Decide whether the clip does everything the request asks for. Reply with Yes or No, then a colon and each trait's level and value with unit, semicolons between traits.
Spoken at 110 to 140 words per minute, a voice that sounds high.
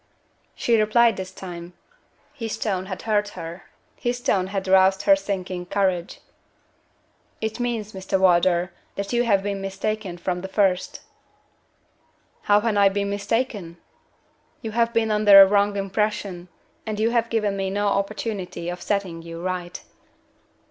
No: average, 150 wpm; high, 200 Hz